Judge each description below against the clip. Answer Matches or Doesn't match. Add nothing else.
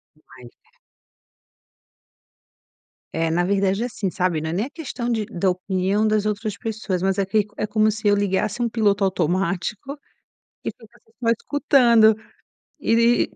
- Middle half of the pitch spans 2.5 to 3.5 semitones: Matches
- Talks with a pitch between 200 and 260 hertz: Matches